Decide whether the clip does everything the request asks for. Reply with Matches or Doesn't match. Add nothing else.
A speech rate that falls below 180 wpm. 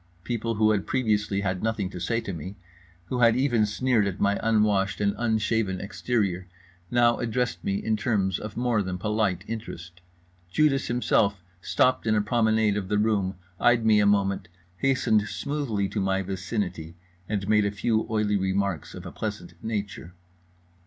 Matches